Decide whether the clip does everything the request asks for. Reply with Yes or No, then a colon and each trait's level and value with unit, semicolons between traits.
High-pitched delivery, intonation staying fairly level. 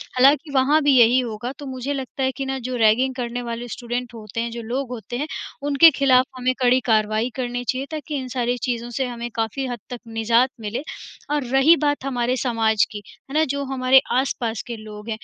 Yes: very high, 250 Hz; narrow, 2.3 semitones